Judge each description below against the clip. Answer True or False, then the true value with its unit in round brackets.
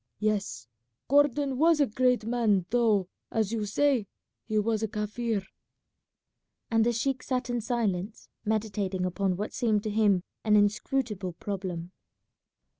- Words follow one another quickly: False (135 wpm)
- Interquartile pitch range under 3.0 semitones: False (3.3 semitones)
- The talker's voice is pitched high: True (215 Hz)